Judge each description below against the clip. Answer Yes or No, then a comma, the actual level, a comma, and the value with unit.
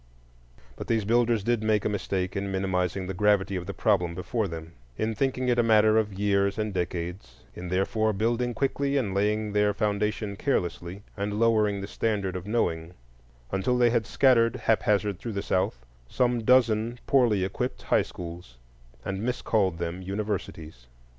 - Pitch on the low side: Yes, low, 105 Hz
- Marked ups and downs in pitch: No, average, 3.2 semitones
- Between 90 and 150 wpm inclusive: No, average, 165 wpm